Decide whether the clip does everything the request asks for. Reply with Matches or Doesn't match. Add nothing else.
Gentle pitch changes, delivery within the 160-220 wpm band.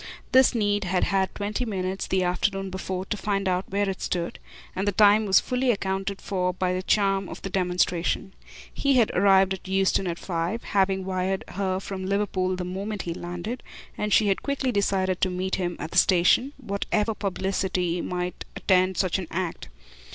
Matches